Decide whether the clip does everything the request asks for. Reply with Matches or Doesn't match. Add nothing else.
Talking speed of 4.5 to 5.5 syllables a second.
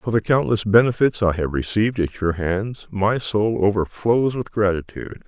Matches